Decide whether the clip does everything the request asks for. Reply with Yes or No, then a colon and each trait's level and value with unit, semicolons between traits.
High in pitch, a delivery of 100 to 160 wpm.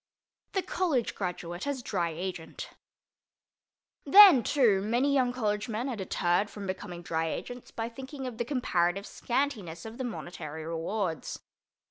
Yes: high, 215 Hz; average, 140 wpm